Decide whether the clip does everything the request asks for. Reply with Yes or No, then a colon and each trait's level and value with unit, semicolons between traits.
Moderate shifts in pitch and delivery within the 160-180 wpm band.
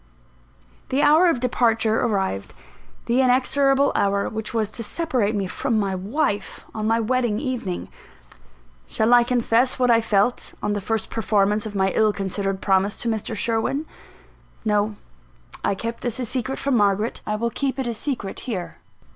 Yes: average, 3.5 semitones; average, 165 wpm